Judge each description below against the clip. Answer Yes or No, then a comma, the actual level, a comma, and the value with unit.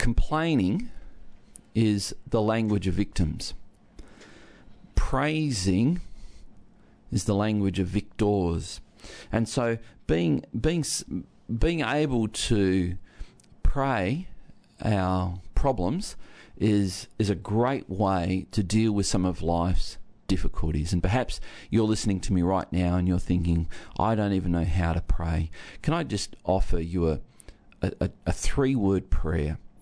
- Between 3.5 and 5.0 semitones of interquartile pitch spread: Yes, average, 4.1 semitones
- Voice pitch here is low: Yes, low, 100 Hz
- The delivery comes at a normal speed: No, slow, 125 wpm